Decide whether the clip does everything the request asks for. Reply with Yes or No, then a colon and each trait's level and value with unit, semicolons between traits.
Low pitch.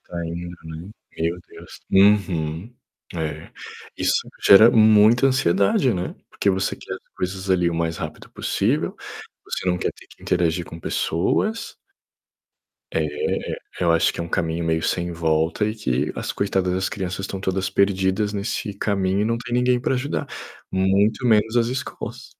Yes: very low, 95 Hz